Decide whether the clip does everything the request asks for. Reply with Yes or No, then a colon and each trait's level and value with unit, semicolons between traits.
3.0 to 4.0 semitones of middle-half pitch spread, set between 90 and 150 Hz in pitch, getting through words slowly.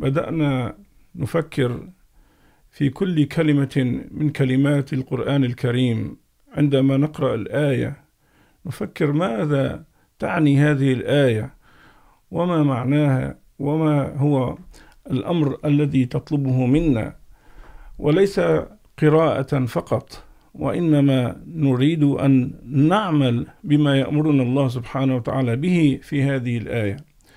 No: narrow, 2.4 semitones; medium, 140 Hz; slow, 90 wpm